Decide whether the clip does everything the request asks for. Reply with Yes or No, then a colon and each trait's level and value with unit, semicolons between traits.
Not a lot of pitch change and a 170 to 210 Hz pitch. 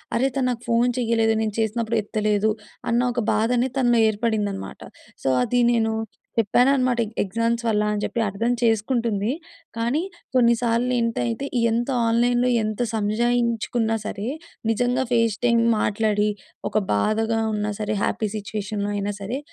No: narrow, 2.1 semitones; high, 230 Hz